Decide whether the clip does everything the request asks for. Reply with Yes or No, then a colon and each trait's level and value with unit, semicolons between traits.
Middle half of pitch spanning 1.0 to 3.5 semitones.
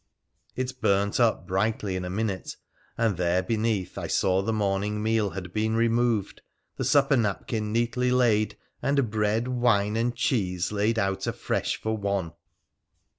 Yes: average, 2.9 semitones